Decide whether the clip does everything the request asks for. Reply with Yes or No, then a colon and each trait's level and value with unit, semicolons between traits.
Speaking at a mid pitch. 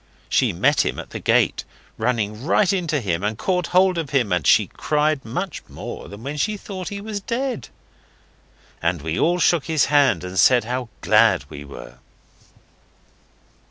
Yes: medium, 145 Hz